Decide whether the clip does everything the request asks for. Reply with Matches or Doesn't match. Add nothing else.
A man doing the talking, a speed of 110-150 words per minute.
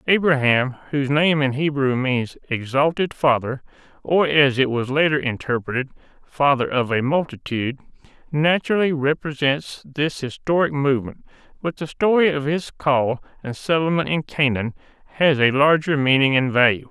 Matches